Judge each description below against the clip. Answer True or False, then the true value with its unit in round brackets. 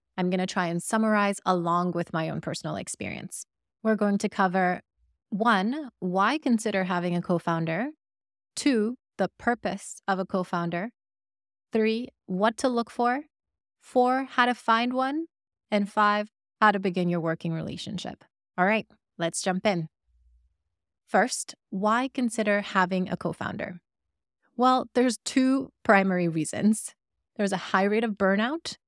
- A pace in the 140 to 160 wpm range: True (145 wpm)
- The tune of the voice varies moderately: True (4.6 semitones)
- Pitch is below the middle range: False (205 Hz)